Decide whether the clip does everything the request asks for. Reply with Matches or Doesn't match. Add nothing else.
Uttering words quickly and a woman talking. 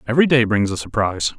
Doesn't match